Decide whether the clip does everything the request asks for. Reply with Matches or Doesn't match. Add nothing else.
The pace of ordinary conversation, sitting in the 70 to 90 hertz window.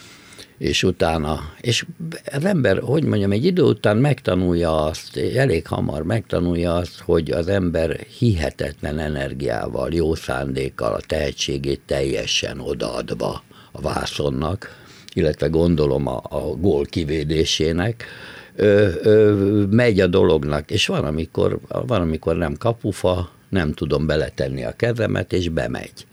Matches